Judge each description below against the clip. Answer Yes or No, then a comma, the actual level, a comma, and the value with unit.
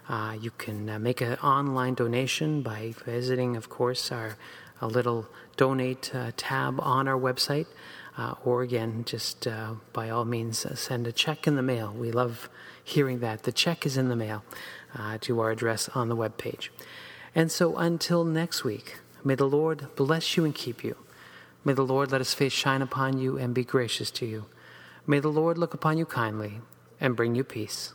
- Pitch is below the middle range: Yes, low, 125 Hz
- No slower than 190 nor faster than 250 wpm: Yes, average, 195 wpm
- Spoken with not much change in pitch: No, average, 3.4 semitones